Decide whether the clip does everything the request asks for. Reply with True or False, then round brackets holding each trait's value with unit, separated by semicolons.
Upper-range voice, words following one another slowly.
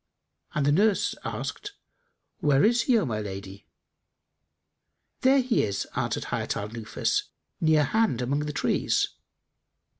False (150 Hz; 130 wpm)